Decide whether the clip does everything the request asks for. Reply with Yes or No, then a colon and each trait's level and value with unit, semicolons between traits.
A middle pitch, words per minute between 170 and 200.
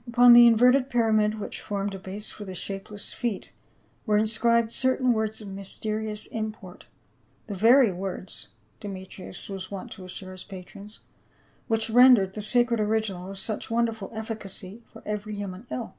No: high, 215 Hz; average, 175 wpm